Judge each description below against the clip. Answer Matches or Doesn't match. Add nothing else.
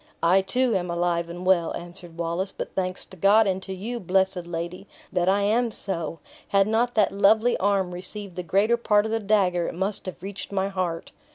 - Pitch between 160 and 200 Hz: Matches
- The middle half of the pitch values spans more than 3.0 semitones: Doesn't match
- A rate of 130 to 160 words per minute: Doesn't match